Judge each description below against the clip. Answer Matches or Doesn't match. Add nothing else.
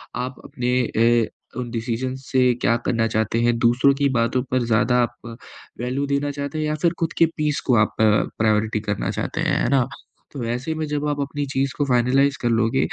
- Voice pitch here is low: Matches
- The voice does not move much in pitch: Doesn't match